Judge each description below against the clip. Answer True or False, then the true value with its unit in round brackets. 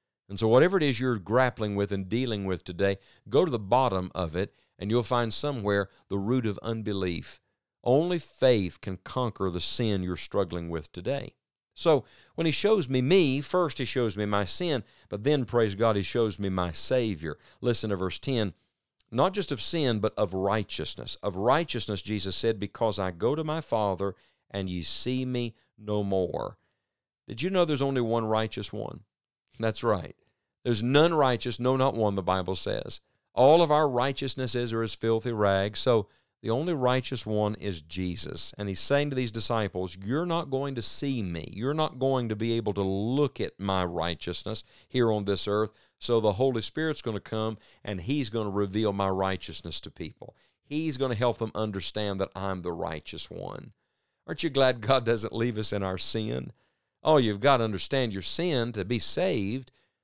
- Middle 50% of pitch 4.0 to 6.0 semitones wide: True (4.5 semitones)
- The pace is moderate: True (195 wpm)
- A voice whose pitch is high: False (110 Hz)